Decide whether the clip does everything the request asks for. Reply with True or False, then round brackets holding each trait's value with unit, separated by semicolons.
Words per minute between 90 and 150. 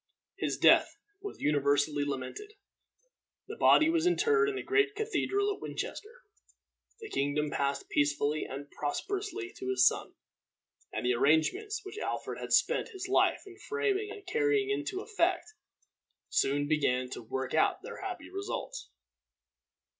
True (140 wpm)